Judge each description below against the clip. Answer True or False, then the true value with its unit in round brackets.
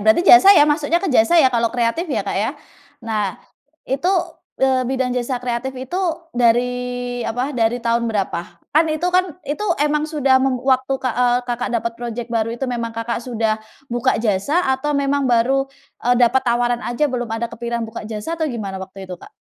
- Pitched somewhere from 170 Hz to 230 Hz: False (245 Hz)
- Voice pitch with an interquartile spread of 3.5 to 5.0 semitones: False (2.7 semitones)